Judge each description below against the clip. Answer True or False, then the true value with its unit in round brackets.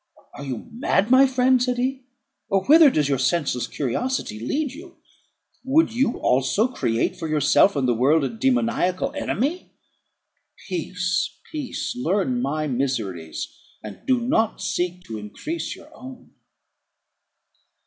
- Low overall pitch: False (190 Hz)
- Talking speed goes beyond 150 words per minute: False (135 wpm)